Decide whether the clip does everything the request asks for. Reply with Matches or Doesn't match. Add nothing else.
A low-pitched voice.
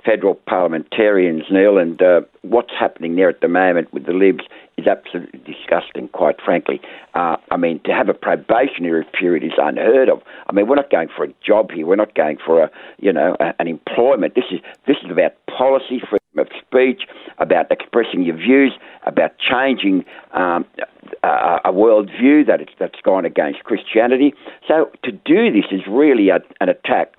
Matches